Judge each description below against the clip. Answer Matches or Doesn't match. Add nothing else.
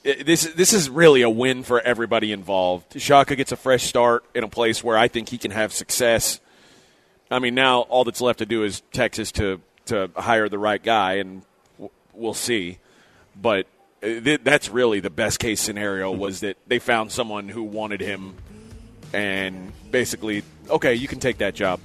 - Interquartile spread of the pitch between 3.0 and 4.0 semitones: Matches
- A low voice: Matches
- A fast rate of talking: Doesn't match